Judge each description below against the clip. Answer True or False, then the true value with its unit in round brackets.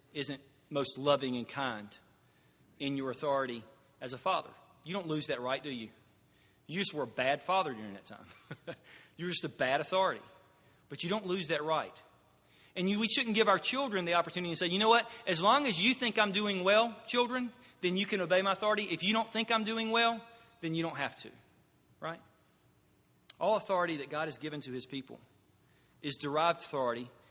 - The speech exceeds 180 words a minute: True (200 wpm)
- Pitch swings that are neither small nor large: False (7.2 semitones)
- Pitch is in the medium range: True (165 Hz)